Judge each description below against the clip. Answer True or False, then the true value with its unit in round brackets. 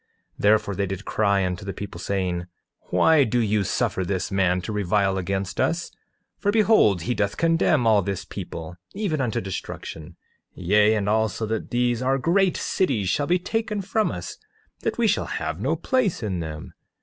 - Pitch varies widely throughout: True (6.9 semitones)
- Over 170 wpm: True (180 wpm)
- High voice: False (105 Hz)